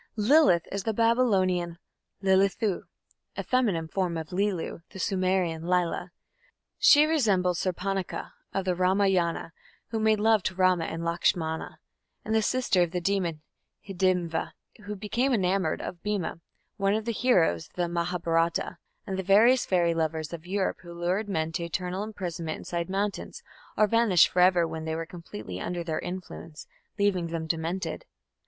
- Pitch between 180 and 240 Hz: Yes, medium, 185 Hz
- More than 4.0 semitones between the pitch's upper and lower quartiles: No, average, 3.1 semitones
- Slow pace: No, average, 155 wpm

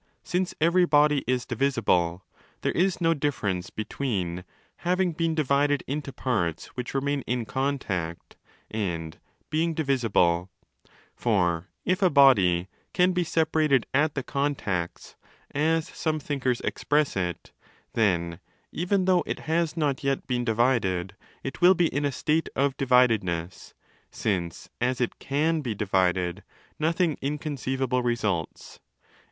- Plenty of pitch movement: Yes, wide, 7.7 semitones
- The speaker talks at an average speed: No, slow, 130 wpm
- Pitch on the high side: No, low, 135 Hz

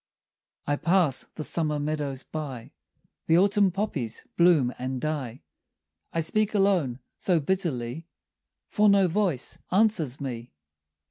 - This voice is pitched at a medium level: Yes, medium, 155 Hz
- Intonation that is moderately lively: No, wide, 6.2 semitones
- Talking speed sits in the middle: No, slow, 120 wpm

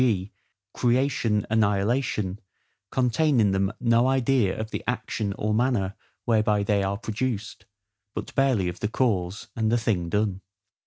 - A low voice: Yes, low, 110 Hz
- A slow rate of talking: No, average, 145 wpm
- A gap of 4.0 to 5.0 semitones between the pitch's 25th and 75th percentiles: No, average, 3.6 semitones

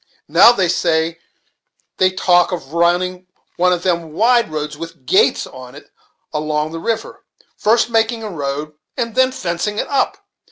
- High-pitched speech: No, medium, 180 Hz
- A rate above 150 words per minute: Yes, average, 160 wpm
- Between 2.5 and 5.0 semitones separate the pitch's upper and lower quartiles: No, wide, 5.4 semitones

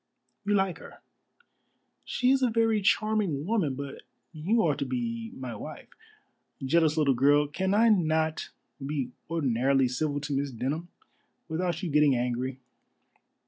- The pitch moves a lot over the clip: Yes, wide, 6.5 semitones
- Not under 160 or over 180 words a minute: No, average, 140 wpm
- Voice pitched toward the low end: No, medium, 155 Hz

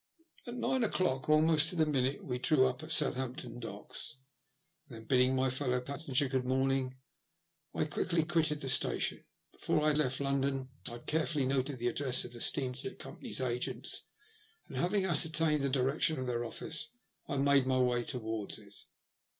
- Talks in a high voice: No, low, 135 Hz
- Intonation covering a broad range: No, average, 3.3 semitones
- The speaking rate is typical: Yes, average, 170 wpm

